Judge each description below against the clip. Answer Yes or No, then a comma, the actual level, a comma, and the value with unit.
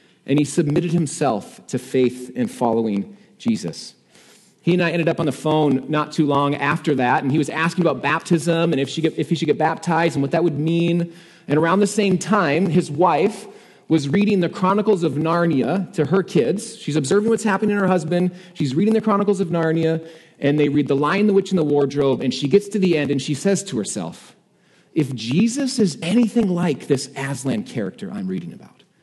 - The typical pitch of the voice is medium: Yes, medium, 165 Hz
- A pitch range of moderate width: Yes, average, 4.8 semitones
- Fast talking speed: Yes, fast, 215 wpm